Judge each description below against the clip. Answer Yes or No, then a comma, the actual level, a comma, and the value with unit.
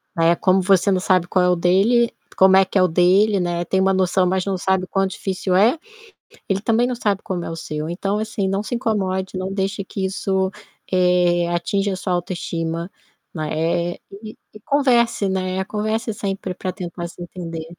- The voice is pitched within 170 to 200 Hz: Yes, high, 190 Hz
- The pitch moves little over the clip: Yes, narrow, 2.1 semitones